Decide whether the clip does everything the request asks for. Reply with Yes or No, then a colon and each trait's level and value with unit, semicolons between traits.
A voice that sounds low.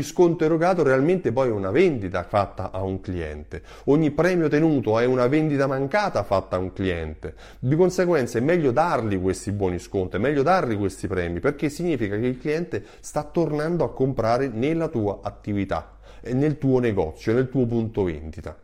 Yes: low, 120 Hz